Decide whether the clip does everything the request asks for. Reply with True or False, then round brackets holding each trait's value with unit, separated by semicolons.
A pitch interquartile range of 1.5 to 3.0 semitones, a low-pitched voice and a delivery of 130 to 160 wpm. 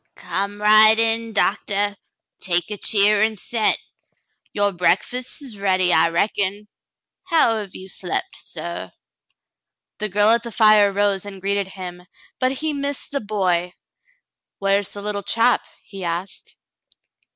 False (2.5 semitones; 205 Hz; 145 wpm)